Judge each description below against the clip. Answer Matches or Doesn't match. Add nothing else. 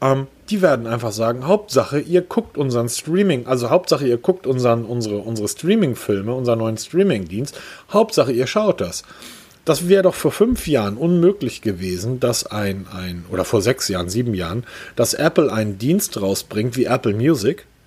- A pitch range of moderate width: Doesn't match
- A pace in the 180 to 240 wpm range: Doesn't match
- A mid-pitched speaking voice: Doesn't match